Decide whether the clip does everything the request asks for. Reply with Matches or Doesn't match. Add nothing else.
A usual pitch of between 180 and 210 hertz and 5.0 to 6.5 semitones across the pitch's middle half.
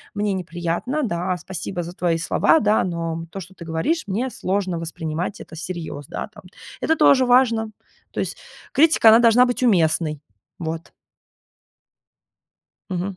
Matches